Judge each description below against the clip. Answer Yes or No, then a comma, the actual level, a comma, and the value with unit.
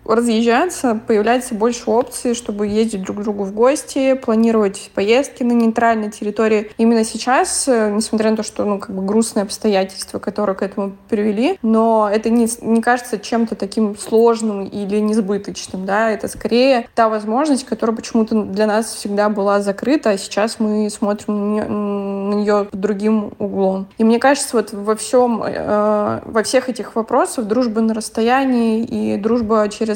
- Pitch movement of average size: No, narrow, 2.0 semitones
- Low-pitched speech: No, high, 220 Hz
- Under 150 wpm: No, fast, 160 wpm